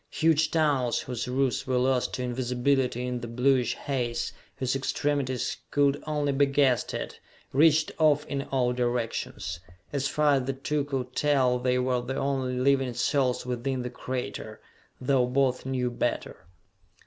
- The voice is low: Yes, low, 130 Hz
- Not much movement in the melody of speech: Yes, narrow, 2.0 semitones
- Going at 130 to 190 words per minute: Yes, average, 155 wpm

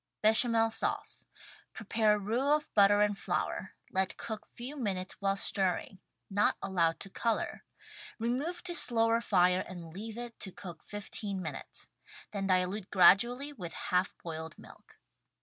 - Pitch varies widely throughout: No, average, 3.7 semitones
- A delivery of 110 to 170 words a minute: Yes, average, 150 wpm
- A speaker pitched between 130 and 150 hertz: No, high, 205 Hz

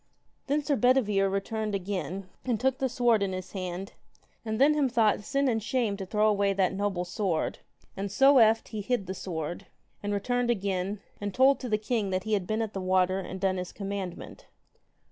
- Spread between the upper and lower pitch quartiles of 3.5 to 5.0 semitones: Yes, average, 3.9 semitones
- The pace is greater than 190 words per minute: Yes, average, 200 wpm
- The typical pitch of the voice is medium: No, high, 205 Hz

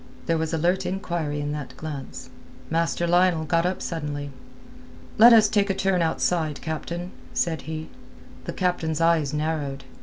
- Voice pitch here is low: No, medium, 165 Hz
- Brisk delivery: No, average, 150 wpm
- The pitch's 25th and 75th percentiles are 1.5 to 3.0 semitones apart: Yes, average, 2.7 semitones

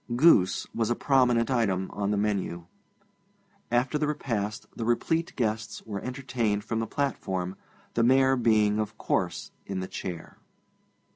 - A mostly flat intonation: No, average, 3.8 semitones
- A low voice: Yes, low, 115 Hz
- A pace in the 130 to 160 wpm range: Yes, average, 145 wpm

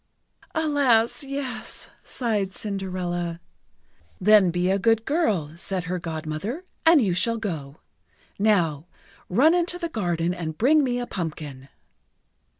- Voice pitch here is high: Yes, high, 195 Hz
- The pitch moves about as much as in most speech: No, wide, 6.4 semitones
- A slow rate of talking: Yes, slow, 125 wpm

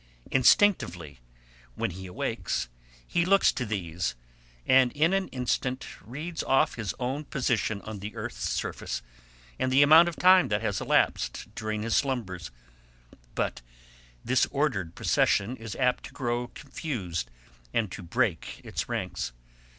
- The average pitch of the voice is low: Yes, low, 120 Hz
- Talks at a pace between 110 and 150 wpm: Yes, average, 140 wpm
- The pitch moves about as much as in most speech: No, wide, 6.2 semitones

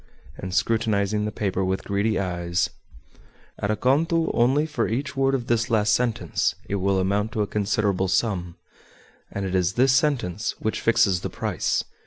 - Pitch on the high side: No, low, 105 Hz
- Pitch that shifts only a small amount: No, average, 3.8 semitones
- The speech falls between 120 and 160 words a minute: No, average, 170 wpm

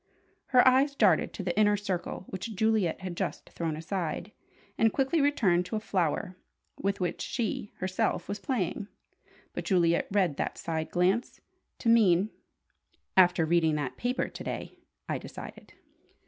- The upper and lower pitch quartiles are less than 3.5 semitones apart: No, average, 4.2 semitones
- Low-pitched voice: No, high, 190 Hz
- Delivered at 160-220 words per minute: No, average, 150 wpm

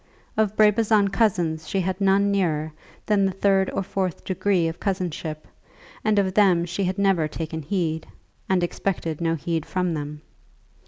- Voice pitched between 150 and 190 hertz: Yes, medium, 185 Hz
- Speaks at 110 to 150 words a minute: No, average, 160 wpm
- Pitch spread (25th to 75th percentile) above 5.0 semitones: No, average, 3.4 semitones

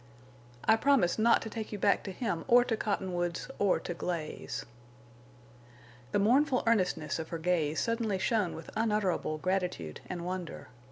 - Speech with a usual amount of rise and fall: Yes, average, 4.3 semitones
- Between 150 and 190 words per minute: Yes, average, 155 wpm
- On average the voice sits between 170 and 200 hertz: Yes, high, 190 Hz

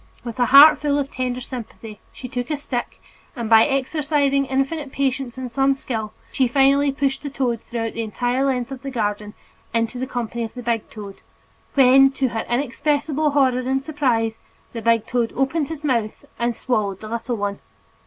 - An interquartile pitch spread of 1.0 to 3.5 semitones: Yes, average, 3.0 semitones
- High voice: Yes, very high, 255 Hz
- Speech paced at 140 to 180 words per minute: No, average, 190 wpm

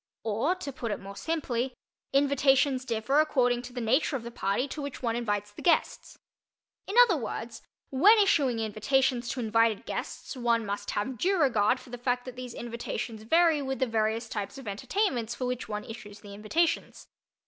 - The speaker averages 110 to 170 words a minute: No, average, 185 wpm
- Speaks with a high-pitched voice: Yes, high, 245 Hz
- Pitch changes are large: No, average, 3.7 semitones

